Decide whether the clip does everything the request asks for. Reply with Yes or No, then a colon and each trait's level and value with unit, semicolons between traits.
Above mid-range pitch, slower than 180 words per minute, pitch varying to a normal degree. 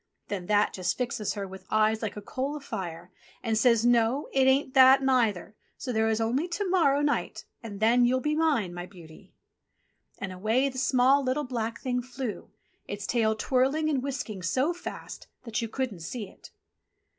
No: high, 240 Hz; average, 185 wpm; average, 4.1 semitones